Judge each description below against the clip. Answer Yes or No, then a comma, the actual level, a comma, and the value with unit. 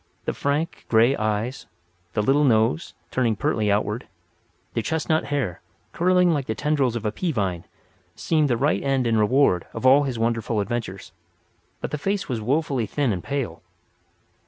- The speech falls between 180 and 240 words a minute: No, average, 165 wpm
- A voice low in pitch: Yes, low, 125 Hz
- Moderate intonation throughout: Yes, average, 4.7 semitones